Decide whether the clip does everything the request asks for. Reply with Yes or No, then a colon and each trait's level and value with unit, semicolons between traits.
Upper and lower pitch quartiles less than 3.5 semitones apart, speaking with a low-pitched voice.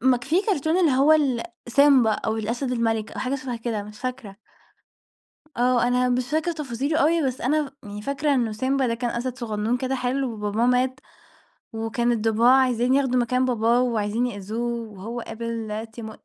No: average, 2.7 semitones; high, 245 Hz